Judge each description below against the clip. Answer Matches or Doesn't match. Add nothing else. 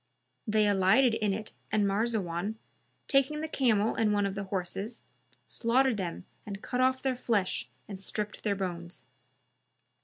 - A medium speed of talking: Matches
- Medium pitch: Doesn't match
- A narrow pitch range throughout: Doesn't match